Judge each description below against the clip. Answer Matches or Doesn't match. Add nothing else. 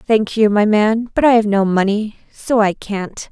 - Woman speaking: Matches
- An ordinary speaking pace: Doesn't match